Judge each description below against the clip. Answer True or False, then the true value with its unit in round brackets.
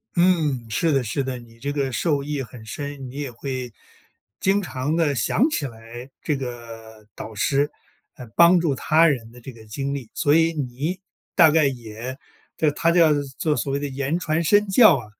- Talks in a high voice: False (140 Hz)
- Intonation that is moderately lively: True (4.7 semitones)